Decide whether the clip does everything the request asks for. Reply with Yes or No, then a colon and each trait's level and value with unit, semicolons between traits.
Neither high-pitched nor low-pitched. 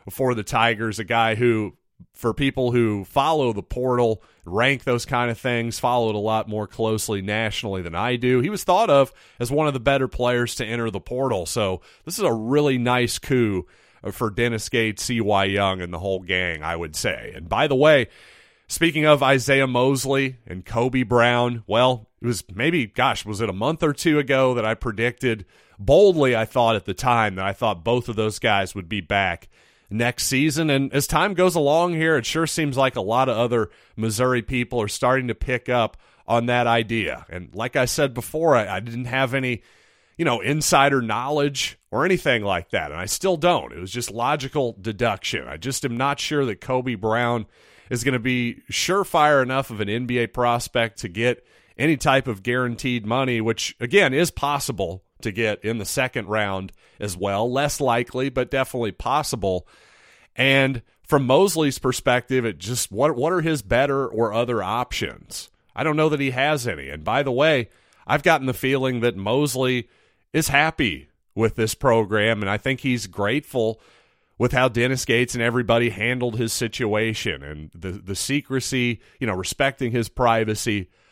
No: low, 120 Hz